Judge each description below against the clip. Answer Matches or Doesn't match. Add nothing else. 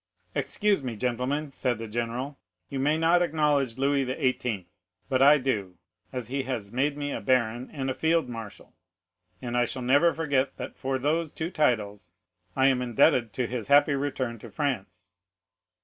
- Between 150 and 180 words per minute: Matches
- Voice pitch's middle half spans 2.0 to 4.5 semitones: Matches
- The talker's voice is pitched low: Matches